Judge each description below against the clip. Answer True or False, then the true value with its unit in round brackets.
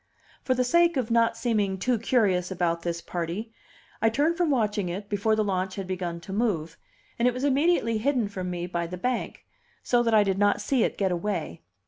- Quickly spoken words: True (210 wpm)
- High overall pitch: True (210 Hz)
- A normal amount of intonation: True (4.9 semitones)